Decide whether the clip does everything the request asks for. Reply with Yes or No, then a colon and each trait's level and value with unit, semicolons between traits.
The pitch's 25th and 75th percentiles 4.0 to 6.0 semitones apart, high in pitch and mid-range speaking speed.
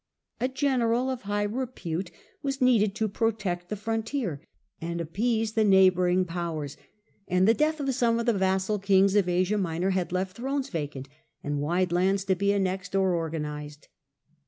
Yes: average, 4.3 semitones; high, 195 Hz; average, 170 wpm